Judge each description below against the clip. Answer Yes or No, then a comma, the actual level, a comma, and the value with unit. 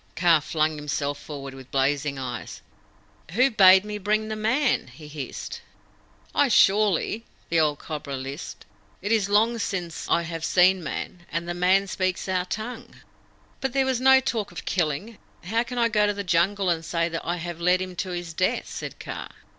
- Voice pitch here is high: No, medium, 180 Hz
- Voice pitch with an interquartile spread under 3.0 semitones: No, average, 5.0 semitones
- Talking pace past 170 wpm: Yes, average, 185 wpm